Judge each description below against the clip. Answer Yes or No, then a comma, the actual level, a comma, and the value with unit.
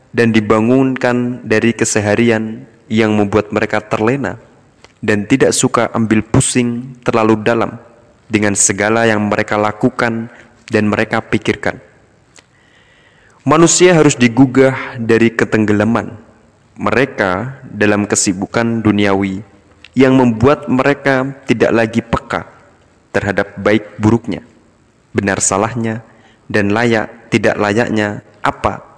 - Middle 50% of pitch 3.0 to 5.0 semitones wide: No, narrow, 2.6 semitones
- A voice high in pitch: No, low, 115 Hz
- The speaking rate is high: No, average, 100 wpm